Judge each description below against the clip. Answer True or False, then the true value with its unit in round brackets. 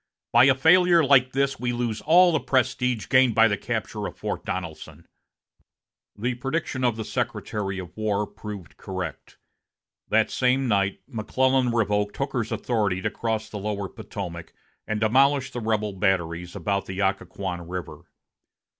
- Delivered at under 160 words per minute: True (150 wpm)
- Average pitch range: True (4.7 semitones)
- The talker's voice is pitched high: False (110 Hz)